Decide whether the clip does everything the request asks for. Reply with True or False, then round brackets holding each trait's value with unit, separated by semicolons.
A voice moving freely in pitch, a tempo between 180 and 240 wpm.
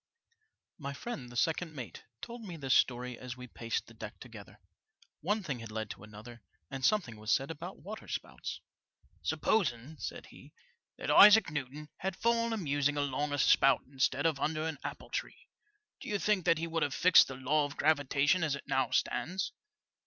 True (5.7 semitones; 185 wpm)